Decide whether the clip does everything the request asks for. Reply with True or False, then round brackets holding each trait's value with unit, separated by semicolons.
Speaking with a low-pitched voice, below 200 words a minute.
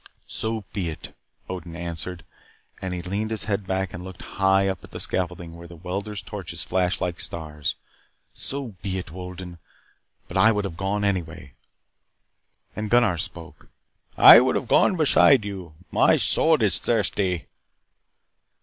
True (95 Hz; 155 wpm)